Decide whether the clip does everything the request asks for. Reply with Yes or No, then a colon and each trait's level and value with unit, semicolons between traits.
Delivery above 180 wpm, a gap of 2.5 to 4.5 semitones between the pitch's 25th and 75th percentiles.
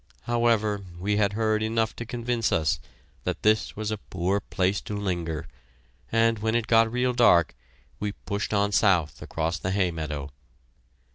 No: average, 160 wpm; average, 3.9 semitones